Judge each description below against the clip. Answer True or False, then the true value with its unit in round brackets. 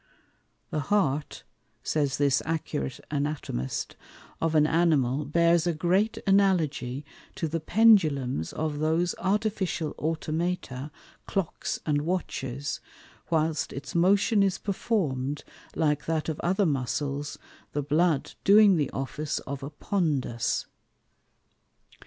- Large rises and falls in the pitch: False (3.9 semitones)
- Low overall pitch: False (155 Hz)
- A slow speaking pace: True (110 wpm)